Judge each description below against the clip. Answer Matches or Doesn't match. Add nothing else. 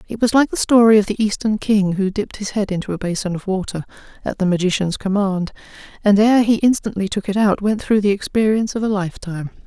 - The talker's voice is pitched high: Matches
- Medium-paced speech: Doesn't match